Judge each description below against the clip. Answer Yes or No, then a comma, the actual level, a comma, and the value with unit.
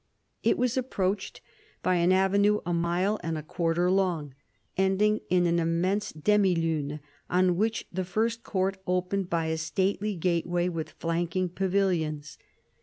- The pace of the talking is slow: No, average, 145 wpm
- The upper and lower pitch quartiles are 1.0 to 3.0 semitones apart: Yes, average, 2.7 semitones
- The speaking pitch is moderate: Yes, medium, 180 Hz